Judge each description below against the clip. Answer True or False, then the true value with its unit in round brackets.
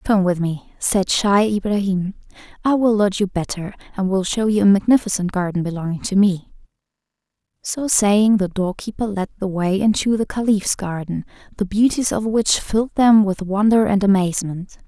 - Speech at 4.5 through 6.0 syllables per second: True (5.1 syllables/s)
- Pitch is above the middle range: True (200 Hz)